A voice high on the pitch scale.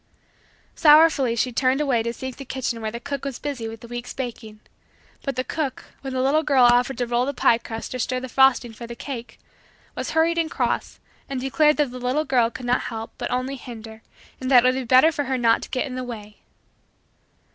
Yes: very high, 255 Hz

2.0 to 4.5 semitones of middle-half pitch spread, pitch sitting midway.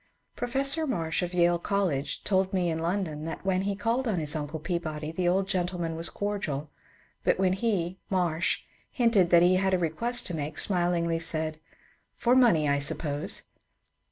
Yes: average, 3.4 semitones; medium, 175 Hz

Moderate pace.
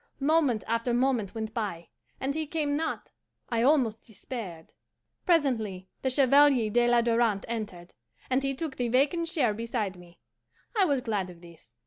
Yes: average, 160 wpm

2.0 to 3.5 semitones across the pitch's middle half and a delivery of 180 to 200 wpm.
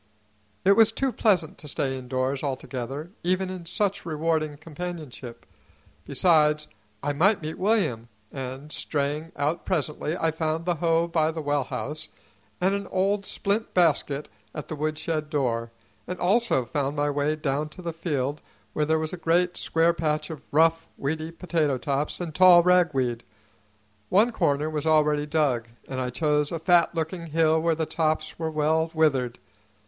No: average, 2.8 semitones; average, 165 wpm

